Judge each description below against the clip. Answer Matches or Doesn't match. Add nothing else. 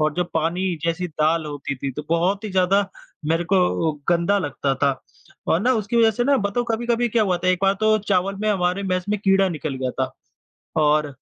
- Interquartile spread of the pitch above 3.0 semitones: Matches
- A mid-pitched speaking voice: Matches